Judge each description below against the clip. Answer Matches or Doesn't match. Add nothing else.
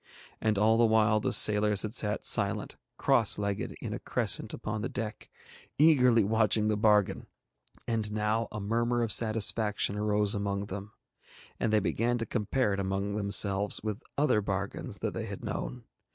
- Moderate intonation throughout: Doesn't match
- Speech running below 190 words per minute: Matches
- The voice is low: Matches